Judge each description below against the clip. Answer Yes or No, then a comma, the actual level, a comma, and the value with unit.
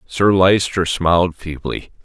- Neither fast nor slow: No, slow, 120 wpm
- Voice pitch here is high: No, very low, 90 Hz